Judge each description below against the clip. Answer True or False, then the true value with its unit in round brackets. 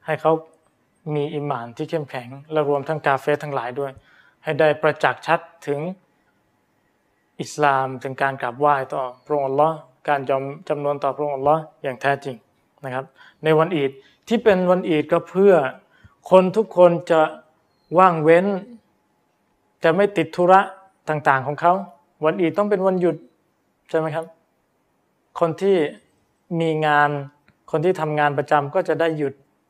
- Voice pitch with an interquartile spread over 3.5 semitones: False (3.1 semitones)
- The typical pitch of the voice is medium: True (155 Hz)